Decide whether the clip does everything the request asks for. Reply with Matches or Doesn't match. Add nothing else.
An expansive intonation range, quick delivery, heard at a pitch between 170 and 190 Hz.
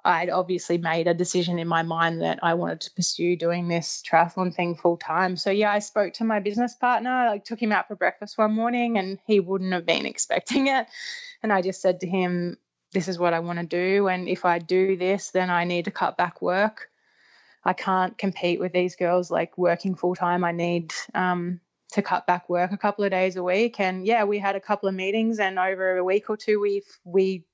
Doesn't match